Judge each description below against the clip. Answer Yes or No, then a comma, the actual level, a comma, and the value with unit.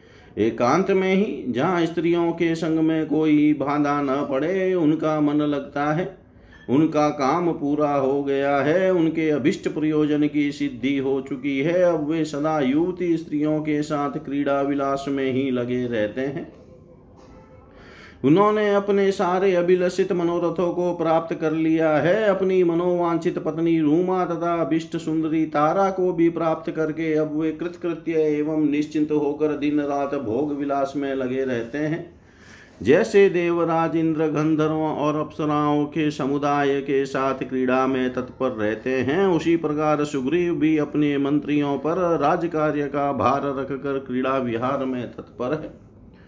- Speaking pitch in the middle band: Yes, medium, 150 Hz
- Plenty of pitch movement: No, average, 3.0 semitones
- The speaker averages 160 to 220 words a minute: No, average, 145 wpm